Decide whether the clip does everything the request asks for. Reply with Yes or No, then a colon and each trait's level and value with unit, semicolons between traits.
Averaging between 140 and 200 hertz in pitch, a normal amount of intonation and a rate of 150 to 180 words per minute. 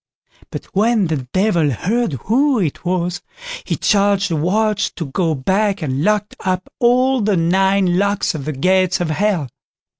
Yes: high, 190 Hz; average, 4.1 semitones; average, 160 wpm